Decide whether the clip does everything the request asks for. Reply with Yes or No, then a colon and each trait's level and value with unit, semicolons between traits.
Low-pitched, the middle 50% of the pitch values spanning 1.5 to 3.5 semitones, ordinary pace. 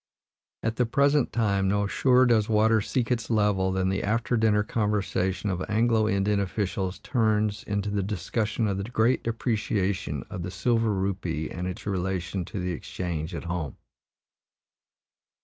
Yes: low, 105 Hz; average, 3.0 semitones; average, 155 wpm